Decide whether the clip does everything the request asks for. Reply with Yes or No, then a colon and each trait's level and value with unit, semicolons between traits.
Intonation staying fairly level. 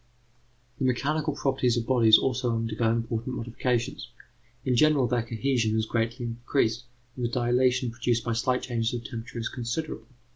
Yes: narrow, 1.8 semitones